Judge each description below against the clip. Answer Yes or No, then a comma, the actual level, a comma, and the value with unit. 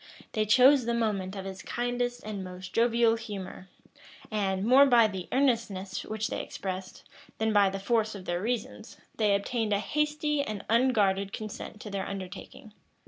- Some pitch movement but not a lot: Yes, average, 3.4 semitones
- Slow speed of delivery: No, average, 165 wpm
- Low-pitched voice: No, high, 215 Hz